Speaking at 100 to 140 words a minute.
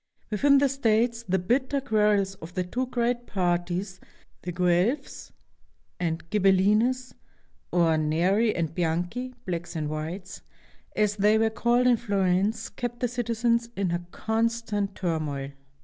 Yes: slow, 135 wpm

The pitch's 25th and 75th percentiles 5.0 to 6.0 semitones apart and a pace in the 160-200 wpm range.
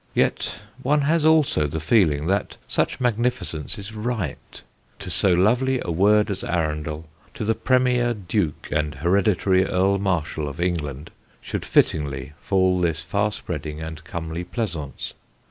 No: wide, 5.4 semitones; average, 145 wpm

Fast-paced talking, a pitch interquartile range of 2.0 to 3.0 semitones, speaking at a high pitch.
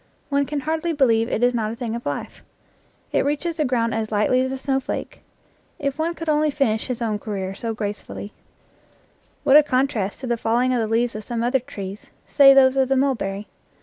No: fast, 210 wpm; average, 3.9 semitones; very high, 250 Hz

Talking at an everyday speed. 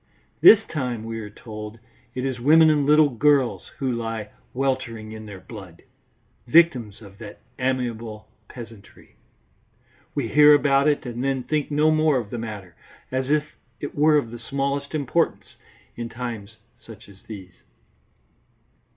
Yes: average, 150 wpm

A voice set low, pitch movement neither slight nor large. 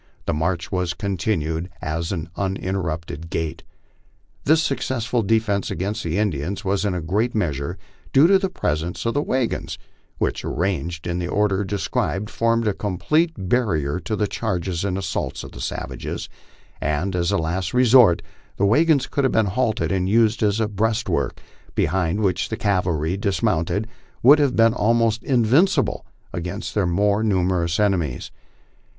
Yes: low, 100 Hz; average, 4.7 semitones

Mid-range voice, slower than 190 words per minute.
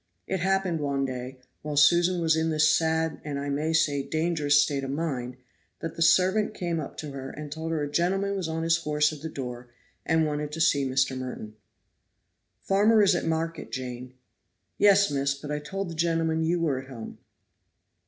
No: medium, 155 Hz; average, 195 wpm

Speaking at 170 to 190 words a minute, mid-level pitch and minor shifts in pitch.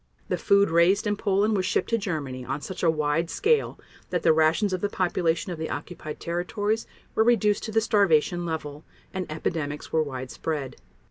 No: average, 185 wpm; medium, 170 Hz; average, 4.4 semitones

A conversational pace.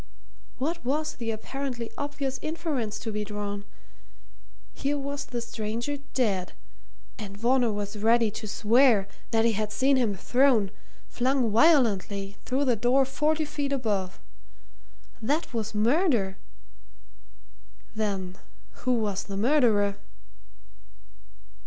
No: slow, 115 wpm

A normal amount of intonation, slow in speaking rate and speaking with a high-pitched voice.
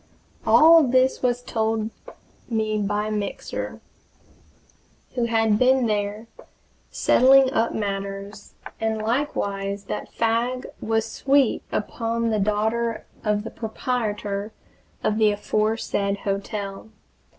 No: narrow, 2.2 semitones; slow, 105 wpm; high, 220 Hz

